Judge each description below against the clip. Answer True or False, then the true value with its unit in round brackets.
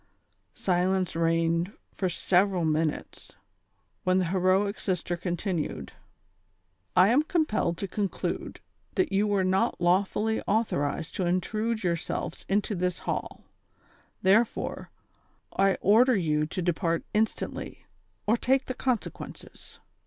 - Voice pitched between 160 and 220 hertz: True (185 Hz)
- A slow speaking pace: True (115 wpm)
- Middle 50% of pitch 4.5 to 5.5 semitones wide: False (3.4 semitones)